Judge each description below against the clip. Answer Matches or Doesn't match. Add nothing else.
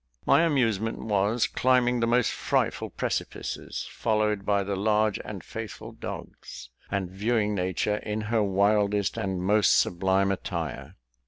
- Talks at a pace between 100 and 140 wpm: Matches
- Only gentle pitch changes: Matches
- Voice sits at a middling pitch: Doesn't match